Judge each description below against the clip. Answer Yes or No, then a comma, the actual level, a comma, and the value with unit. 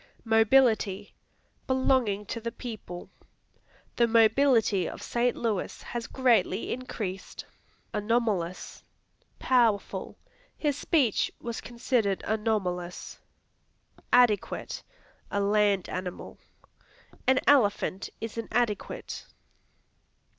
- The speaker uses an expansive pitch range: No, average, 3.2 semitones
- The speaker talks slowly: Yes, slow, 85 wpm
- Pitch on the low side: No, high, 225 Hz